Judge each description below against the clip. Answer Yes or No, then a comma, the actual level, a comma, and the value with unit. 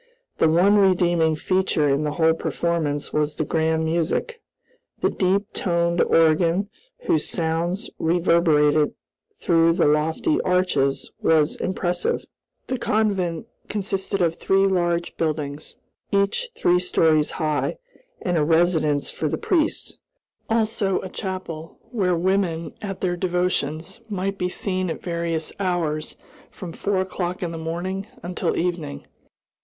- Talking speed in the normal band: No, slow, 130 wpm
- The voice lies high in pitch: No, medium, 175 Hz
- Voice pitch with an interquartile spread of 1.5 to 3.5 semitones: Yes, average, 2.9 semitones